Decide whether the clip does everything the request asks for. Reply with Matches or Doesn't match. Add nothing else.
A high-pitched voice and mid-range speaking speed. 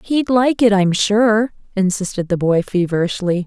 Matches